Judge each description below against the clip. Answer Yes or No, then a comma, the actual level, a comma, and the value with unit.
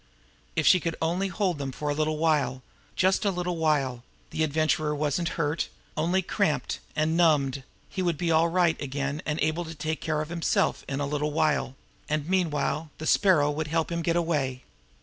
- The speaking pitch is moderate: Yes, medium, 155 Hz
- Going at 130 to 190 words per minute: No, average, 200 wpm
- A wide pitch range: No, narrow, 2.4 semitones